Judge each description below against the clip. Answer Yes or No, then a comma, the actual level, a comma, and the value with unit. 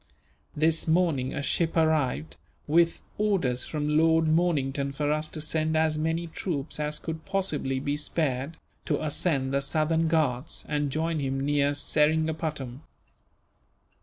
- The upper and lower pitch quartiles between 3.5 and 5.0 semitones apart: No, narrow, 2.4 semitones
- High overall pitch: No, medium, 155 Hz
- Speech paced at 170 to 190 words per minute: No, slow, 135 wpm